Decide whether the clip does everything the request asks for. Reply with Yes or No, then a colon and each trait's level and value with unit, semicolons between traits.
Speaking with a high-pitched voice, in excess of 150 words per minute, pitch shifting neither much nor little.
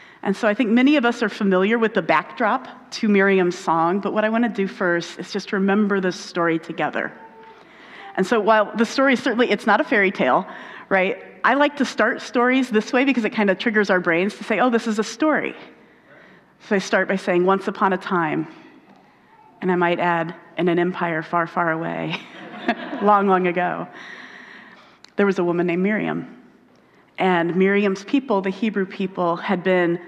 Yes: high, 200 Hz; average, 195 wpm; average, 3.9 semitones